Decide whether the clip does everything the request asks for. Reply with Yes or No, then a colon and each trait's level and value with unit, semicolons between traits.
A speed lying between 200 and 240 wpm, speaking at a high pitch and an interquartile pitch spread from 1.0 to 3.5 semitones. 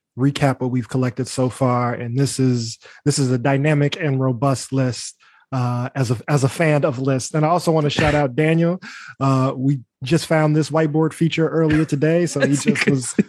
No: fast, 205 wpm; medium, 140 Hz; average, 3.2 semitones